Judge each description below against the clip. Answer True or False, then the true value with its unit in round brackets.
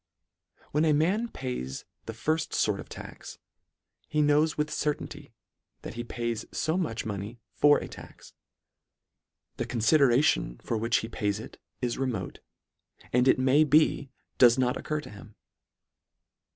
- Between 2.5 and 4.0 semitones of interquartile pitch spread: False (4.8 semitones)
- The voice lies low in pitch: True (130 Hz)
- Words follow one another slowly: False (145 wpm)